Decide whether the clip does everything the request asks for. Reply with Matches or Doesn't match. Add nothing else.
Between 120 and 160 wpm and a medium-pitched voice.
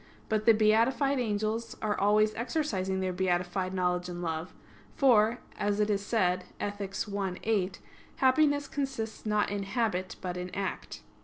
Doesn't match